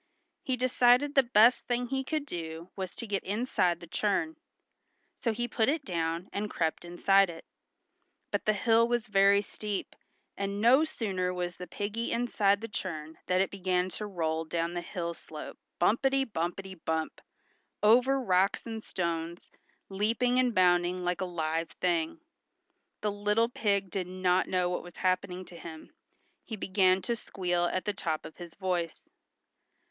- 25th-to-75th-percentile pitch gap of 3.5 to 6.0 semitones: Yes, average, 4.3 semitones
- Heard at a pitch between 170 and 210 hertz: Yes, high, 190 Hz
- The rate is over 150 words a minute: Yes, average, 165 wpm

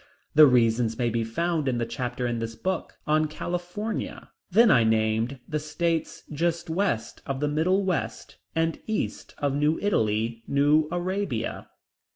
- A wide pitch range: Yes, wide, 6.6 semitones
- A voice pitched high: No, medium, 150 Hz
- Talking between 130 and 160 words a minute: Yes, average, 155 wpm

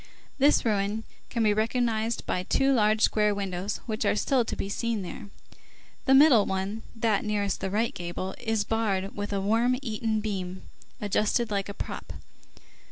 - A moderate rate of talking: Yes, average, 165 wpm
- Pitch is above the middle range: Yes, high, 215 Hz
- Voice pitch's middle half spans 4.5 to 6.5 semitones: No, narrow, 2.4 semitones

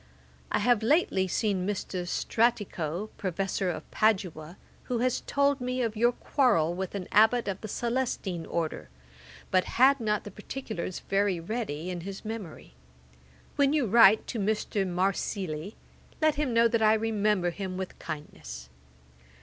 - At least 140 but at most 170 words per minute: Yes, average, 150 wpm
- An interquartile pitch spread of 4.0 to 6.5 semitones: Yes, average, 4.4 semitones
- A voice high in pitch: Yes, high, 205 Hz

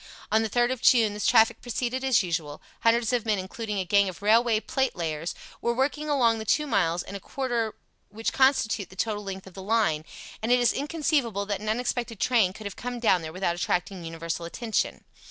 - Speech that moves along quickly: Yes, fast, 210 wpm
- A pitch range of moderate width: Yes, average, 4.3 semitones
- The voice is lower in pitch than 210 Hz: No, high, 220 Hz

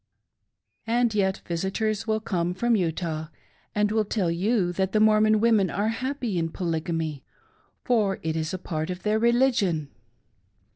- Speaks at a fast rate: No, average, 150 wpm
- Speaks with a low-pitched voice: No, high, 195 Hz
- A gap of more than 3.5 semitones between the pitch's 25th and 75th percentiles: Yes, average, 4.4 semitones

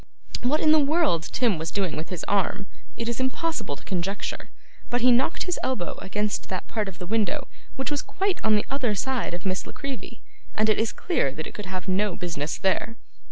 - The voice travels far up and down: Yes, wide, 6.0 semitones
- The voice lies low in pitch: No, high, 210 Hz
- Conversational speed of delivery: No, fast, 215 wpm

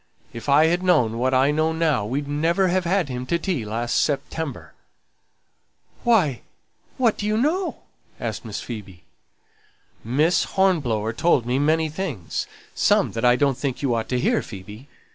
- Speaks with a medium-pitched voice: Yes, medium, 145 Hz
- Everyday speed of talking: Yes, average, 160 wpm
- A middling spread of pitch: No, wide, 6.1 semitones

